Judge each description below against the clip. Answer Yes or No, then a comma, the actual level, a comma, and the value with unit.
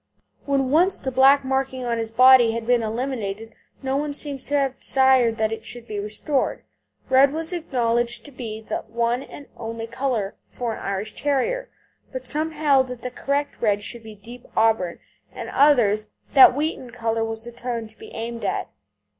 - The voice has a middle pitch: No, high, 245 Hz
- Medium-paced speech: Yes, average, 185 wpm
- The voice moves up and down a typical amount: Yes, average, 3.4 semitones